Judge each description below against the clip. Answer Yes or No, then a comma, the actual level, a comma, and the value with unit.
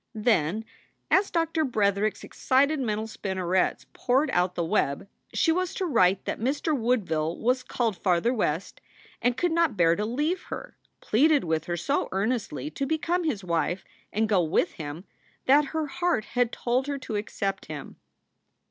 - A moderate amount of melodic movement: No, wide, 7.7 semitones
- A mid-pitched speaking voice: No, high, 225 Hz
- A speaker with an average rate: Yes, average, 165 wpm